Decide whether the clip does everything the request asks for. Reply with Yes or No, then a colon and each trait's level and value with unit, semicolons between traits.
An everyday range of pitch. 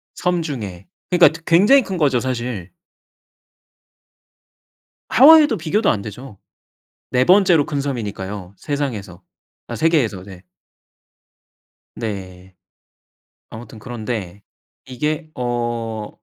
No: wide, 7.4 semitones